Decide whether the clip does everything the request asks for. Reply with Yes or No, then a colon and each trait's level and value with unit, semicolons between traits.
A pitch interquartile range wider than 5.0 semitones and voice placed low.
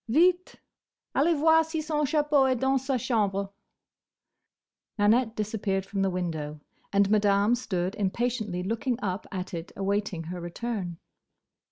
No: wide, 5.6 semitones; high, 210 Hz